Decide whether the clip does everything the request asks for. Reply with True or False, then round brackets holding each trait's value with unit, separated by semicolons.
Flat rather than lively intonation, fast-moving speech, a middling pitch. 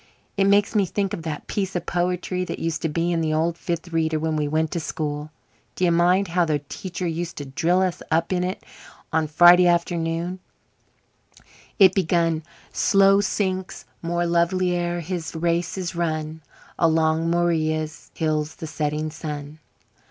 False (2.1 semitones; 165 wpm; 170 Hz)